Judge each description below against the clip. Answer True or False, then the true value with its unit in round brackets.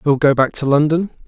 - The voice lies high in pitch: False (145 Hz)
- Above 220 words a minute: True (235 wpm)